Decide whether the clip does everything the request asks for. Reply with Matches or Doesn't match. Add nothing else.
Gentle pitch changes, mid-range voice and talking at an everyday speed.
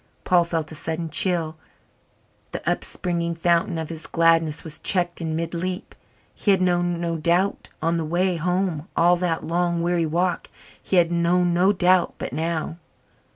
Matches